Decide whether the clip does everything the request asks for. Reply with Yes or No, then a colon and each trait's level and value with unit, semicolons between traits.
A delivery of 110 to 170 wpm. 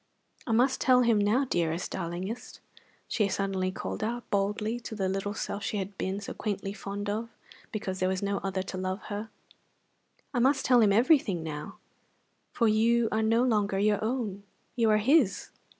No: average, 180 wpm